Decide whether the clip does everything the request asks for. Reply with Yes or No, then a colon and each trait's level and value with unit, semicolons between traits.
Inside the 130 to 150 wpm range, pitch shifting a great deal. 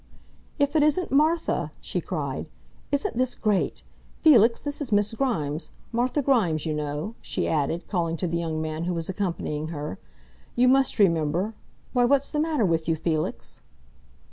No: average, 165 wpm; wide, 8.7 semitones